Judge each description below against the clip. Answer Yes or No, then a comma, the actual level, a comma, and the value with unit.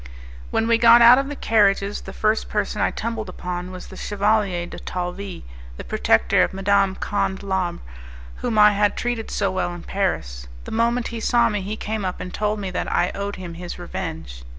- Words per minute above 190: Yes, average, 200 wpm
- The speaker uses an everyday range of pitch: Yes, average, 3.1 semitones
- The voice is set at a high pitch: Yes, high, 200 Hz